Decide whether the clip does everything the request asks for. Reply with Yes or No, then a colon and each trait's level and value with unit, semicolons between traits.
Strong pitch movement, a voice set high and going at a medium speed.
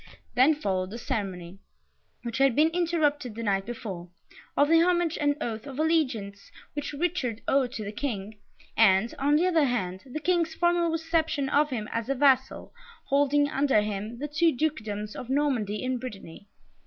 Yes: wide, 6.2 semitones; very high, 265 Hz; average, 170 wpm